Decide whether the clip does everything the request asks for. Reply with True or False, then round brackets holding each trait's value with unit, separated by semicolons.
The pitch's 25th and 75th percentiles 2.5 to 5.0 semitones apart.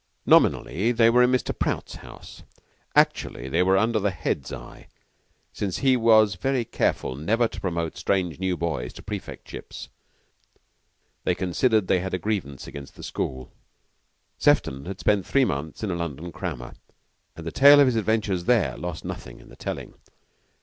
False (5.4 semitones)